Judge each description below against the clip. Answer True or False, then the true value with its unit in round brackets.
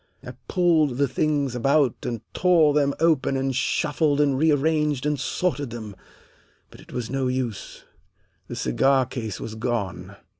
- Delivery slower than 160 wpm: True (150 wpm)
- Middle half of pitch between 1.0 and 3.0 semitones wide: False (3.6 semitones)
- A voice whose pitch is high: False (135 Hz)